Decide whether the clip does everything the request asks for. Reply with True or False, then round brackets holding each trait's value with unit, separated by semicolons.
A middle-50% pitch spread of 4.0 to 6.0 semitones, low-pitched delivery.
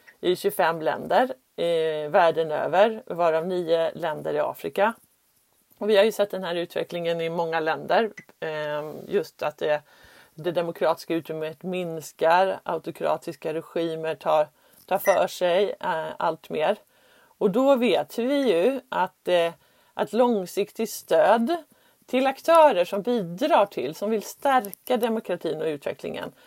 False (5.4 semitones; 180 Hz)